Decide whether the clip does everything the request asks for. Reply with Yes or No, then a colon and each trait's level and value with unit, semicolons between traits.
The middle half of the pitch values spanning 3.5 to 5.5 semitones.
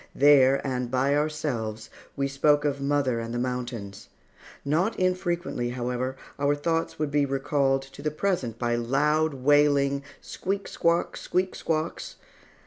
No: average, 3.1 semitones